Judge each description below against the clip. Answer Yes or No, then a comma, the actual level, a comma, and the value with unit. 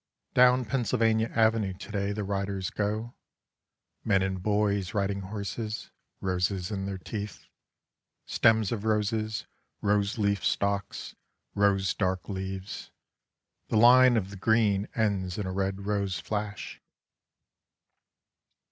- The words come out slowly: Yes, slow, 120 wpm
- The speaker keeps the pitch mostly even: Yes, narrow, 2.2 semitones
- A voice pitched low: Yes, low, 100 Hz